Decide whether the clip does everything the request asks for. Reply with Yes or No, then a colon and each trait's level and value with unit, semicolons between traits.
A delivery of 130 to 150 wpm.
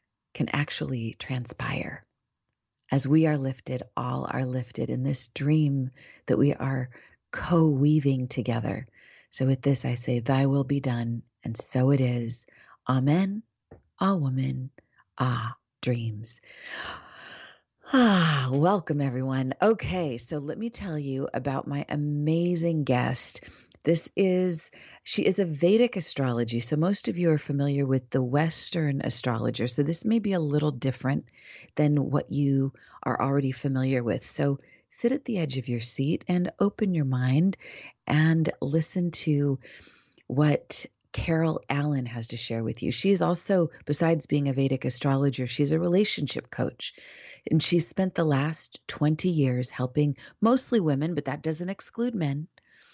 Yes: average, 145 wpm